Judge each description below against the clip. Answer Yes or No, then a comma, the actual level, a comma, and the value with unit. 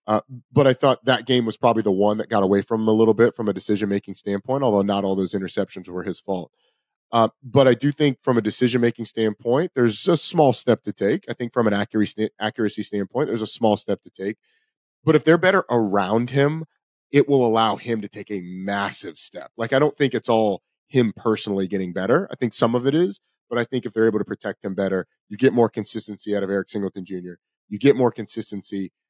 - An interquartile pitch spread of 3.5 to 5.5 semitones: Yes, average, 3.8 semitones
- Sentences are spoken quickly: Yes, fast, 245 wpm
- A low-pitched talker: Yes, low, 110 Hz